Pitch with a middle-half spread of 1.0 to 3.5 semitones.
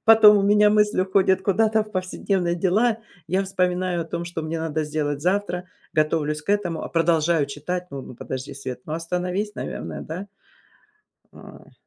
No: average, 4.0 semitones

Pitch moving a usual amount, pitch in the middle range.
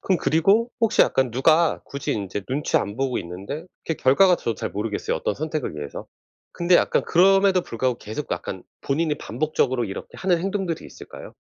No: wide, 7.1 semitones; medium, 150 Hz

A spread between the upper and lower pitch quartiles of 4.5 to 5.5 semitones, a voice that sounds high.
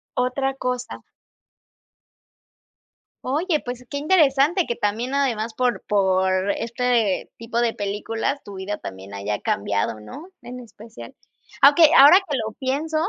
Yes: average, 5.1 semitones; high, 240 Hz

